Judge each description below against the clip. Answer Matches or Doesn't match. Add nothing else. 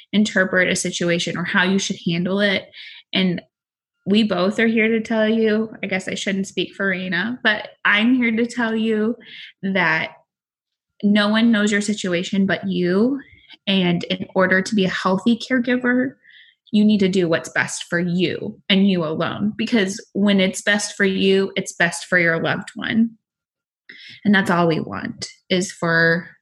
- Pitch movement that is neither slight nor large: Matches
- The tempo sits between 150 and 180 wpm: Matches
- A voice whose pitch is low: Doesn't match